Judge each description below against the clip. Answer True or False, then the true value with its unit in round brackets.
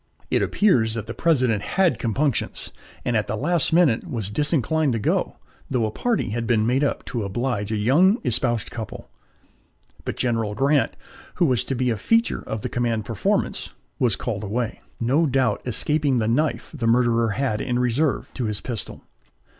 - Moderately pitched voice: False (120 Hz)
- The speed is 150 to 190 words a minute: True (180 wpm)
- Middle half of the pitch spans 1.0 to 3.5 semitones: False (4.1 semitones)